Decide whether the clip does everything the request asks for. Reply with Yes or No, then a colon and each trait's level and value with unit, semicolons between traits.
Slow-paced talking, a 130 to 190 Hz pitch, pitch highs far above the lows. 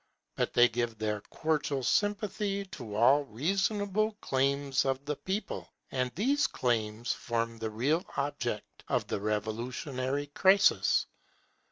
Yes: slow, 125 wpm; low, 135 Hz; wide, 8.2 semitones